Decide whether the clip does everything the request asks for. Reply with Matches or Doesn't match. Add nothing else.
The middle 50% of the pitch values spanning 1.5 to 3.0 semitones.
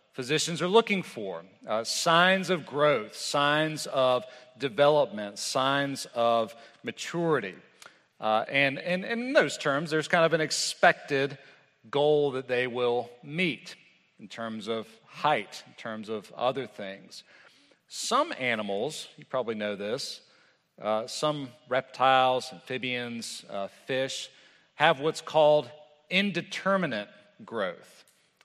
Doesn't match